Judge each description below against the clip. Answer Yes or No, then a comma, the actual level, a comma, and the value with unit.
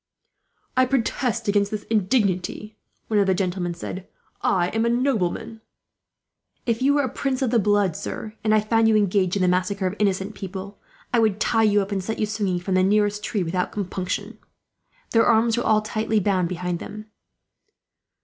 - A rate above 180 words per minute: Yes, average, 190 wpm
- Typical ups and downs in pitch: Yes, average, 3.0 semitones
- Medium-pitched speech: No, high, 210 Hz